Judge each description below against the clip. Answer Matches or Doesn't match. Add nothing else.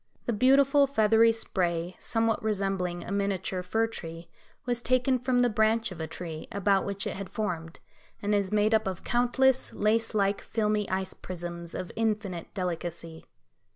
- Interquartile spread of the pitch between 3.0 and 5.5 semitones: Matches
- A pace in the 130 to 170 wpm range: Matches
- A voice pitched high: Matches